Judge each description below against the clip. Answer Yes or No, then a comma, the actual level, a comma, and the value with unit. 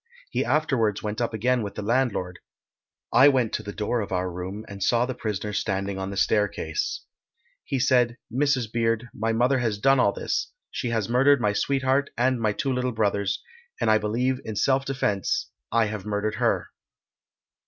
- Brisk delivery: No, average, 185 wpm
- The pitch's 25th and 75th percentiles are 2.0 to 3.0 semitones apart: No, average, 3.8 semitones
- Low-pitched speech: Yes, low, 115 Hz